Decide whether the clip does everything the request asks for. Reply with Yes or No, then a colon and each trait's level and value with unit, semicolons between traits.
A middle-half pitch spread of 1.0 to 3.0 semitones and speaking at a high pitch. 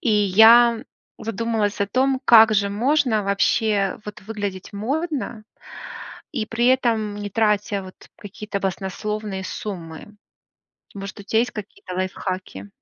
Yes: narrow, 2.4 semitones; high, 210 Hz